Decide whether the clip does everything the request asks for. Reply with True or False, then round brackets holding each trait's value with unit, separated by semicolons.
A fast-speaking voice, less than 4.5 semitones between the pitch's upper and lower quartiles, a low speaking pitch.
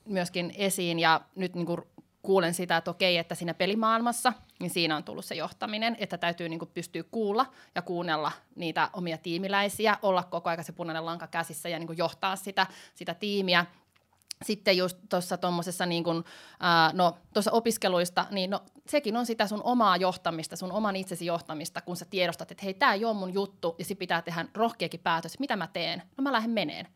False (185 wpm; 2.9 semitones; 180 Hz)